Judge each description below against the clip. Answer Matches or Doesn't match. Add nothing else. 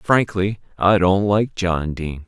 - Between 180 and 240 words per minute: Doesn't match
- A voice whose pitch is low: Matches